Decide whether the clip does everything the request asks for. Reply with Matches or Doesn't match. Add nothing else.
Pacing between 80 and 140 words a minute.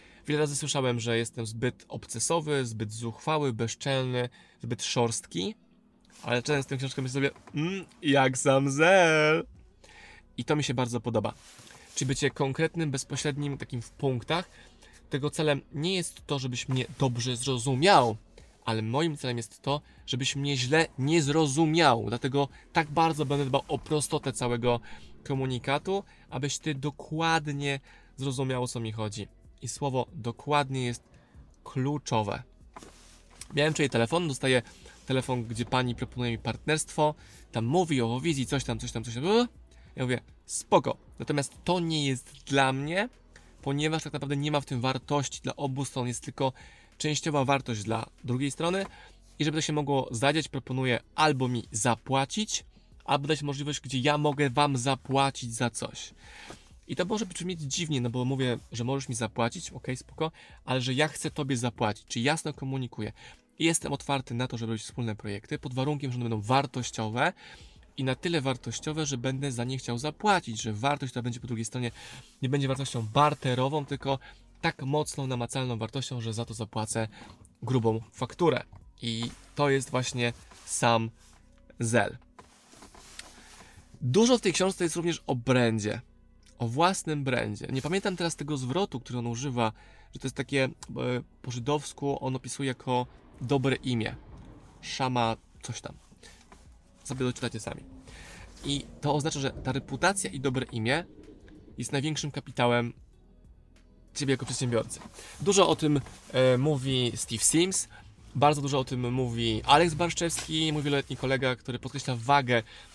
Doesn't match